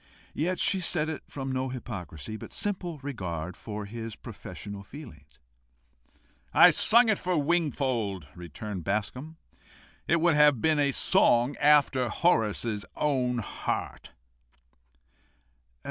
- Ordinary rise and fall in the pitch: No, wide, 6.6 semitones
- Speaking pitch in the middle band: No, low, 130 Hz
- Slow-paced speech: Yes, slow, 120 wpm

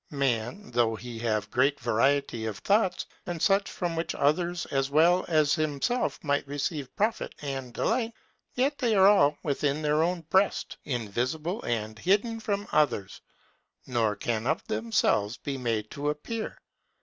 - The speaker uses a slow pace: No, average, 150 wpm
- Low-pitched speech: No, medium, 145 Hz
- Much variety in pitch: Yes, wide, 7.2 semitones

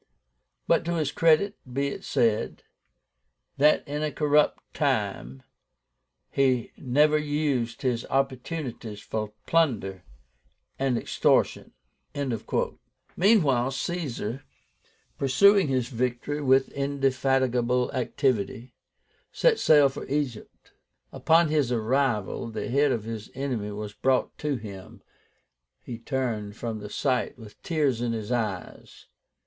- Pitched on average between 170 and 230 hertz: No, low, 130 Hz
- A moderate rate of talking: No, slow, 110 wpm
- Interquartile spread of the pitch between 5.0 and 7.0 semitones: No, average, 4.1 semitones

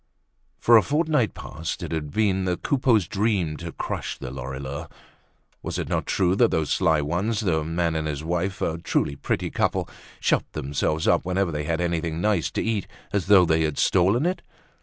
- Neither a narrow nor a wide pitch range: Yes, average, 4.4 semitones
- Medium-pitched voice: No, very low, 85 Hz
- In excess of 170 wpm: Yes, average, 190 wpm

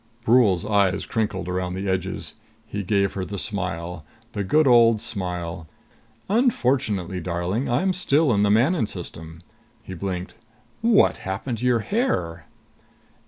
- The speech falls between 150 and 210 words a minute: No, slow, 135 wpm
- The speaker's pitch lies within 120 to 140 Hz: No, low, 100 Hz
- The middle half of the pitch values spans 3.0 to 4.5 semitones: No, average, 5.1 semitones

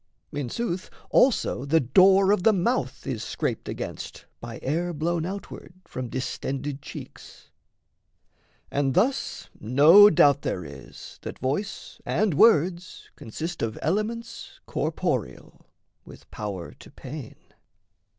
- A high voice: No, medium, 160 Hz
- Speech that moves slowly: Yes, slow, 120 wpm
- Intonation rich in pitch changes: Yes, wide, 6.9 semitones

